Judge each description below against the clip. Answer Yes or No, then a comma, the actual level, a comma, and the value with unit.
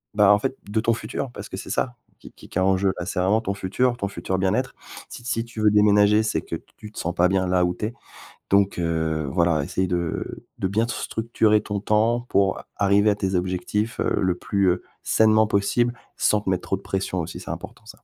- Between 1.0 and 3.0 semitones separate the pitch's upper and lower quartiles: Yes, average, 2.7 semitones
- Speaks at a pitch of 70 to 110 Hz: Yes, low, 100 Hz